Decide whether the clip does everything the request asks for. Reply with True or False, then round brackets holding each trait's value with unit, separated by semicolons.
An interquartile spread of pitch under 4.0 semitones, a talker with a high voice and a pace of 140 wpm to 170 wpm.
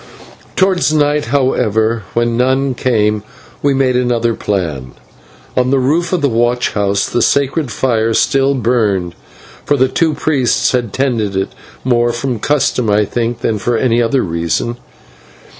False (3.4 semitones; 120 Hz; 150 wpm)